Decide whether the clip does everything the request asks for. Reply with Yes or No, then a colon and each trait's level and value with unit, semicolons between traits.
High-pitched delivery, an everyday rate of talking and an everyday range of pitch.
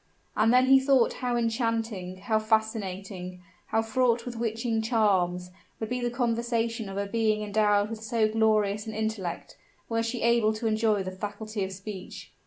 No: high, 220 Hz; average, 170 wpm; narrow, 2.1 semitones